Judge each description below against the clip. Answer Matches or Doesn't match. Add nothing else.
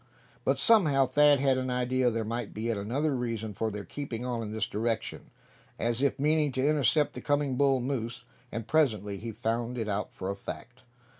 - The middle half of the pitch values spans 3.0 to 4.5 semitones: Matches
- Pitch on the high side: Doesn't match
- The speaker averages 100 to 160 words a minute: Doesn't match